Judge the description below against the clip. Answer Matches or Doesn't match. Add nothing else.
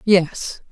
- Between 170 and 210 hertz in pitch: Matches